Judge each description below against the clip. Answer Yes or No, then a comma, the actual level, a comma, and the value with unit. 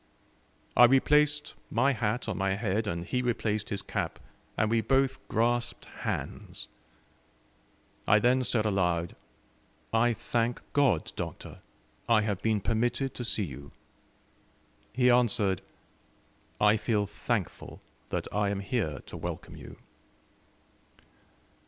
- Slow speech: Yes, slow, 120 wpm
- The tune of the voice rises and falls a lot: No, average, 3.2 semitones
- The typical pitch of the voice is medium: No, low, 110 Hz